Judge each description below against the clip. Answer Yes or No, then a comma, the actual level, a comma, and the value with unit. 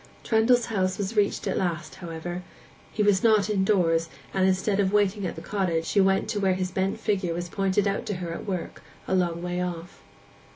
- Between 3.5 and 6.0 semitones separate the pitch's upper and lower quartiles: No, narrow, 2.6 semitones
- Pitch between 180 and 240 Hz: Yes, high, 190 Hz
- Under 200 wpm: No, fast, 205 wpm